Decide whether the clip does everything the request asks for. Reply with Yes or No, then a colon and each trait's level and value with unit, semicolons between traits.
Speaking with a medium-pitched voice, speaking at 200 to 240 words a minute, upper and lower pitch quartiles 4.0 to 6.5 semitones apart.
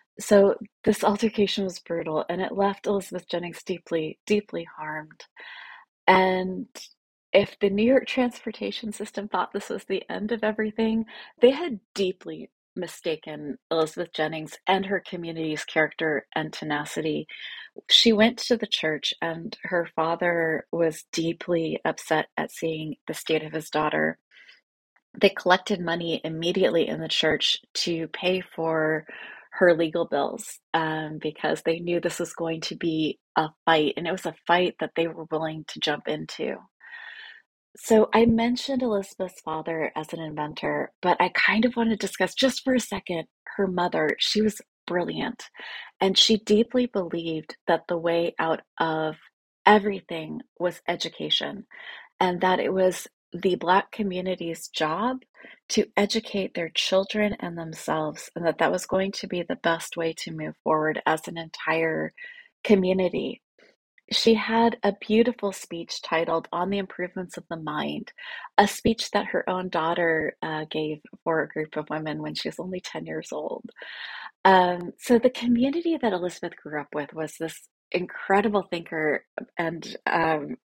No: medium, 180 Hz; average, 155 wpm; average, 4.6 semitones